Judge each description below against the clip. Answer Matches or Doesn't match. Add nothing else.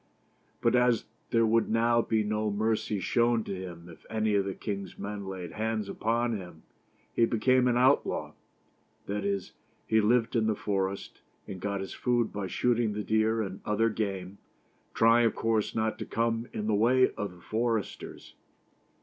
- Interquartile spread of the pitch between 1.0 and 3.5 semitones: Matches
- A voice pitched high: Doesn't match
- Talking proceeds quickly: Doesn't match